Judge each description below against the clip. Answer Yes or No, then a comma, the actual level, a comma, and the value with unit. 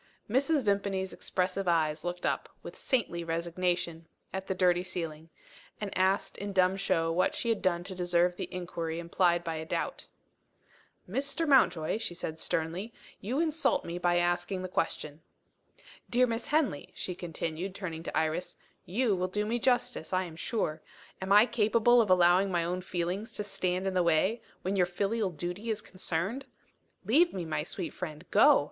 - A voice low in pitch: No, medium, 185 Hz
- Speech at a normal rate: Yes, average, 175 wpm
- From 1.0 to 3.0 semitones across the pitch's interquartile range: No, average, 3.4 semitones